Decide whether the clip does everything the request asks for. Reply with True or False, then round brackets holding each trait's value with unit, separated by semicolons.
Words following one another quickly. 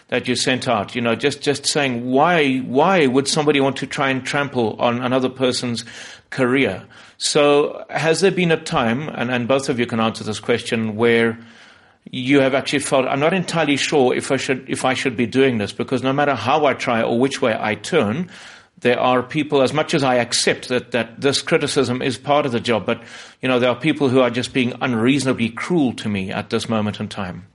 True (220 wpm)